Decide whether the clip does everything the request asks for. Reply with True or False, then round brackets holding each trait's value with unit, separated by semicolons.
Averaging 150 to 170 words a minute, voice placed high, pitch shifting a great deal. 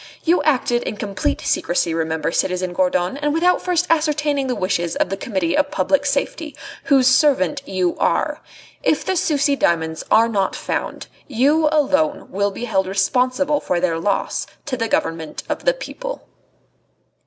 True (160 wpm; 250 Hz; 8.2 semitones)